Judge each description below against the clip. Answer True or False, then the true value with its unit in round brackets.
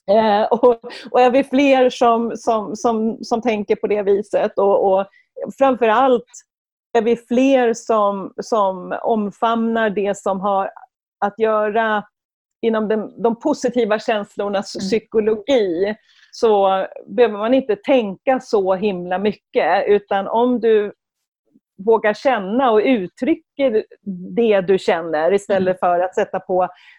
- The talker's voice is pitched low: False (220 Hz)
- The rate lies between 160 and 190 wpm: False (125 wpm)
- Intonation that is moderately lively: True (3.3 semitones)